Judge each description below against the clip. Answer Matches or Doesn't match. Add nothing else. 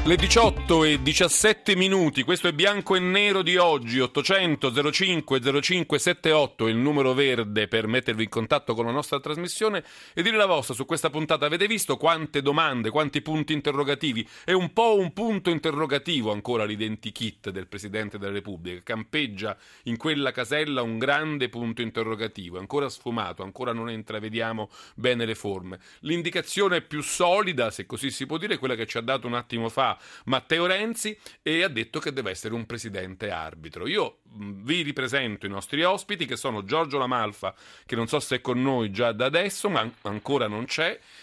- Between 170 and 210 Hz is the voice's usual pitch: Doesn't match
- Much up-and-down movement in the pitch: Matches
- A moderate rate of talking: Doesn't match